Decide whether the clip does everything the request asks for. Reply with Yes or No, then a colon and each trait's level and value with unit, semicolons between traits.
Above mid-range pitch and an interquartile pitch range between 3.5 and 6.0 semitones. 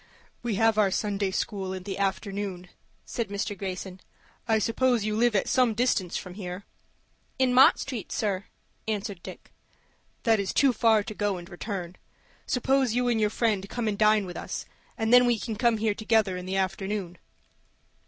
No: high, 210 Hz; average, 2.9 semitones